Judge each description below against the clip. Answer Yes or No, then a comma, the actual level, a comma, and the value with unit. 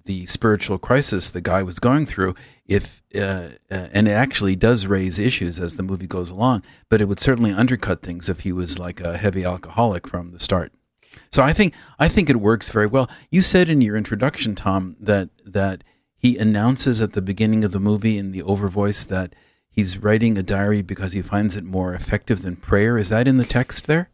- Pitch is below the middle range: Yes, low, 105 Hz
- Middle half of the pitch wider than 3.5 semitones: Yes, average, 4.2 semitones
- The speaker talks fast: Yes, fast, 215 wpm